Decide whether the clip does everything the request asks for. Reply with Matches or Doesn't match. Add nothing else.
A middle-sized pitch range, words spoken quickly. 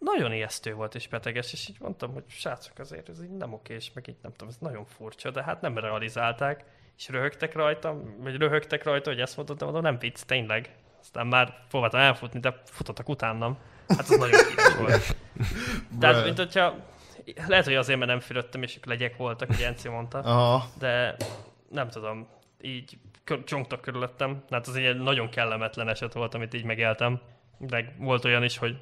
Matches